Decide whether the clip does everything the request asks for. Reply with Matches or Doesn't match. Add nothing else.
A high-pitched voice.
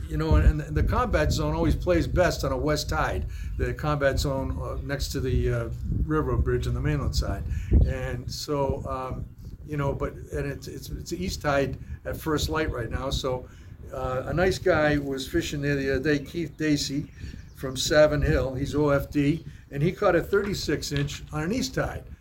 Doesn't match